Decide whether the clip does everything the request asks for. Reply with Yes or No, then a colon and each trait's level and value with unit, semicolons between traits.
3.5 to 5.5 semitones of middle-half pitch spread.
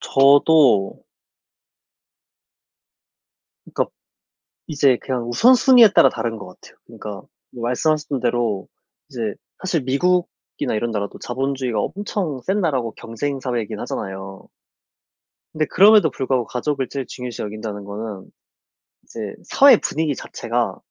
Yes: average, 5.2 semitones